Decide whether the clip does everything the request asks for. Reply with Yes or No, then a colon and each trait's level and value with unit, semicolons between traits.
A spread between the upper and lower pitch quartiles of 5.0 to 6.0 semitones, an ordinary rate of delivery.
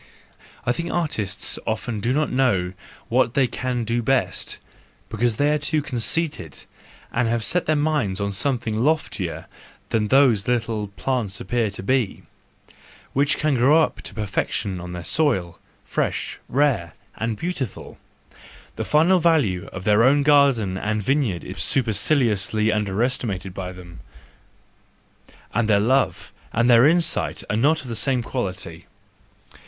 Yes: wide, 5.6 semitones; average, 150 wpm